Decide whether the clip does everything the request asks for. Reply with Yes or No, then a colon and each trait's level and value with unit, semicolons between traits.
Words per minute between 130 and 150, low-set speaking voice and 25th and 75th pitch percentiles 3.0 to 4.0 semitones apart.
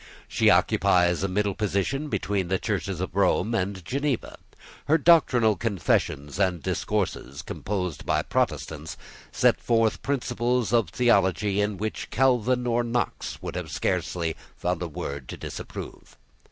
No: average, 140 wpm; low, 100 Hz; average, 4.9 semitones